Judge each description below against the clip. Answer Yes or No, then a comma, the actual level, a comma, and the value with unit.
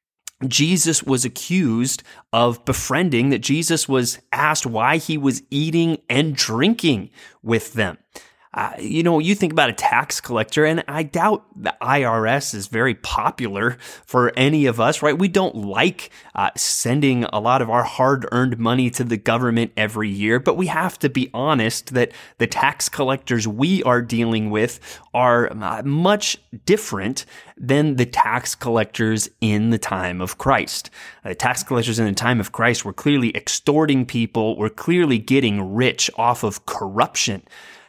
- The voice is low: Yes, low, 125 Hz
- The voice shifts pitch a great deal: No, average, 4.6 semitones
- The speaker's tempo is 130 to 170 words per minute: Yes, average, 165 wpm